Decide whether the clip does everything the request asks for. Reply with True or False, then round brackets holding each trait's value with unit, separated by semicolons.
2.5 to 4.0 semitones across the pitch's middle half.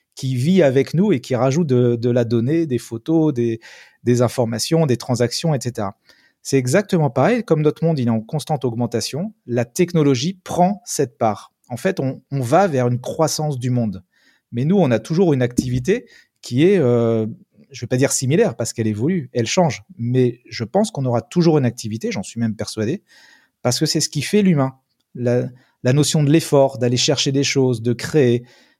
False (4.8 semitones)